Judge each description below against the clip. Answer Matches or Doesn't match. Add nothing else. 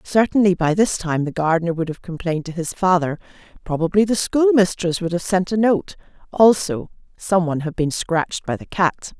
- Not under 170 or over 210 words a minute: Matches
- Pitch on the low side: Doesn't match